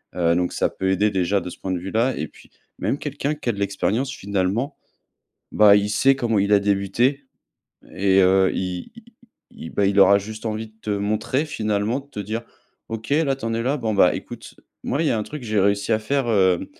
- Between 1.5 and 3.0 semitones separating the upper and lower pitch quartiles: No, average, 3.6 semitones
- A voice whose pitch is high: No, low, 105 Hz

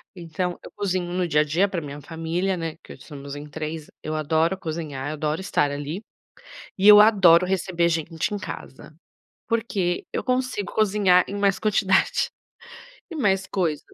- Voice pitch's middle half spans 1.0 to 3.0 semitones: No, average, 3.9 semitones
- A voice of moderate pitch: Yes, medium, 175 Hz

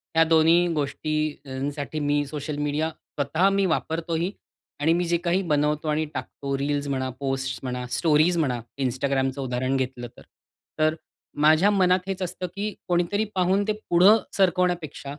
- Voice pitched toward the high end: No, medium, 155 Hz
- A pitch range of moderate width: Yes, average, 3.9 semitones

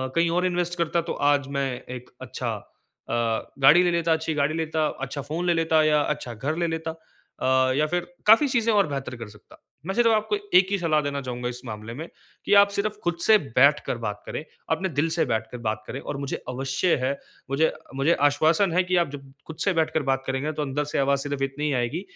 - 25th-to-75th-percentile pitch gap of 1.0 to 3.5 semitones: No, average, 4.2 semitones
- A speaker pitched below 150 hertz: No, medium, 155 Hz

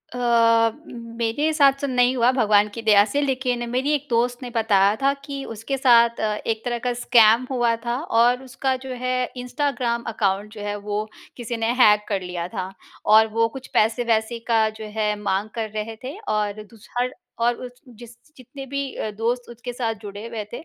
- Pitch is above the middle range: Yes, high, 235 Hz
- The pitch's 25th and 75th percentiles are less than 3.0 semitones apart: Yes, narrow, 2.6 semitones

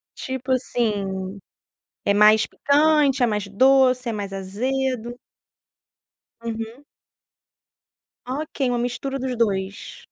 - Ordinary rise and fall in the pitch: Yes, average, 4.1 semitones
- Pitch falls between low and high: No, high, 240 Hz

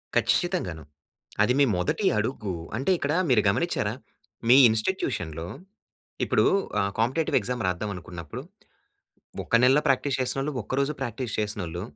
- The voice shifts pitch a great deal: Yes, wide, 6.6 semitones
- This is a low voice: Yes, low, 110 Hz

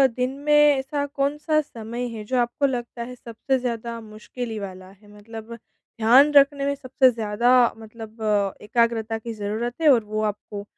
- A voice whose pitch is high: Yes, high, 235 Hz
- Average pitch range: Yes, average, 3.4 semitones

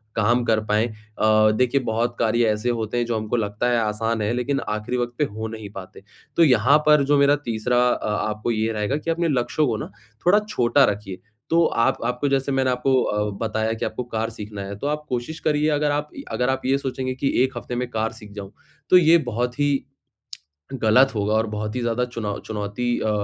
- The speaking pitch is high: No, low, 120 Hz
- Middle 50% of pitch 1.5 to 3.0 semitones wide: No, average, 3.7 semitones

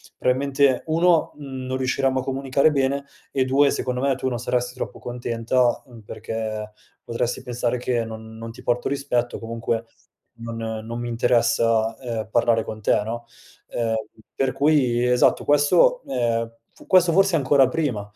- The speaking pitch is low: Yes, low, 125 Hz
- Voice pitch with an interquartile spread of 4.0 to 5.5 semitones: No, average, 2.8 semitones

